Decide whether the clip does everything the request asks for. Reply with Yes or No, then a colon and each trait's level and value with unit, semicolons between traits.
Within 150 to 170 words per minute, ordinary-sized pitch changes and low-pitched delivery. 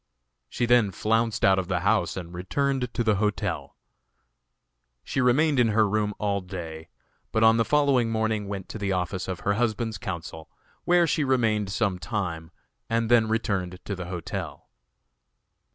Yes: average, 165 wpm; average, 3.8 semitones; low, 105 Hz